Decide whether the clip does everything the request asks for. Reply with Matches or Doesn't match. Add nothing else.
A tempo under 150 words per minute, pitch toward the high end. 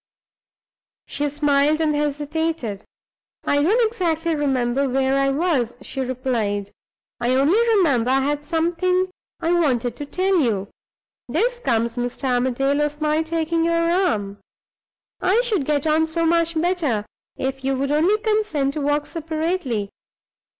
Matches